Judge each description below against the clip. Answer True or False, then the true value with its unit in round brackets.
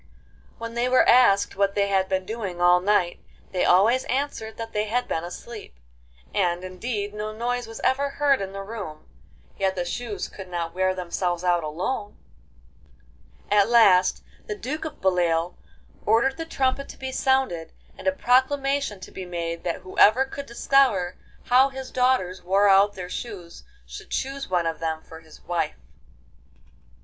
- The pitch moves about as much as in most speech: False (5.8 semitones)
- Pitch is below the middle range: False (200 Hz)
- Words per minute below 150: False (165 wpm)